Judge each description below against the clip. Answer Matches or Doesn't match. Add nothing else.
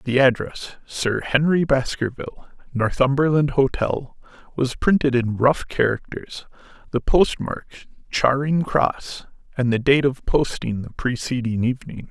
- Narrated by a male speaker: Matches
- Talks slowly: Matches